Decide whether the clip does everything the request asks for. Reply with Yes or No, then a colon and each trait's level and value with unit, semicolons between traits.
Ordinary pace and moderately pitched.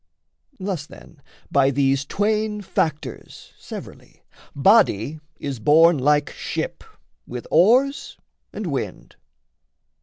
No: slow, 95 wpm; medium, 155 Hz